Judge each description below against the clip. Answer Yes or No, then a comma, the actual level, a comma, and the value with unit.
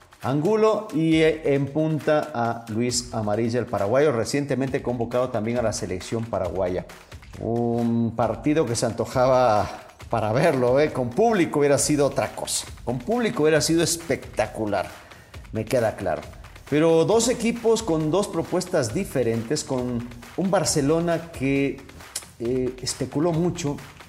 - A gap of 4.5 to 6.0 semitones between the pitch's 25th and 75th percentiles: Yes, average, 5.3 semitones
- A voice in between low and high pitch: No, low, 130 Hz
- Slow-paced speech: Yes, slow, 130 wpm